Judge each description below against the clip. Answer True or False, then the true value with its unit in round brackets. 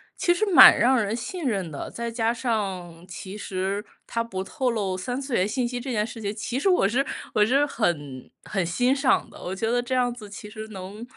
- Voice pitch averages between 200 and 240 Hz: True (225 Hz)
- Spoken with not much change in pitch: False (4.2 semitones)